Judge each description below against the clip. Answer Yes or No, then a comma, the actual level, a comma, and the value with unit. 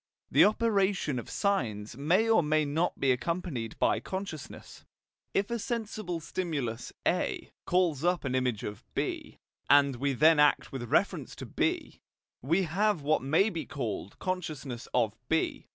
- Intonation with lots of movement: Yes, wide, 6.2 semitones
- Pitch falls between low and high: Yes, medium, 155 Hz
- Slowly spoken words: No, average, 150 wpm